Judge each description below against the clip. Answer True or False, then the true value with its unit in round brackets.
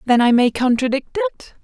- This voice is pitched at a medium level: False (250 Hz)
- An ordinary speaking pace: True (185 wpm)